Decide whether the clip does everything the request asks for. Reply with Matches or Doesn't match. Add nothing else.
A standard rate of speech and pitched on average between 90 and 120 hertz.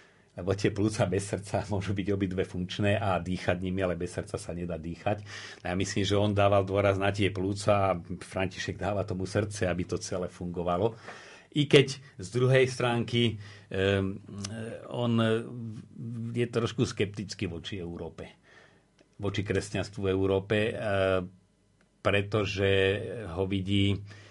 Matches